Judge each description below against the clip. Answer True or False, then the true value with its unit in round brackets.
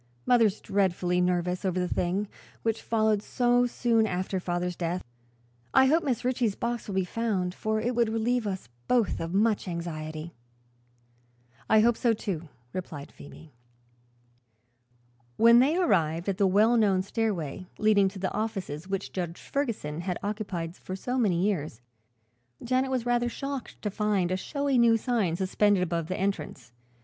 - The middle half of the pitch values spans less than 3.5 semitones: False (4.5 semitones)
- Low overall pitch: False (200 Hz)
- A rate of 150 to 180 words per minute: True (160 wpm)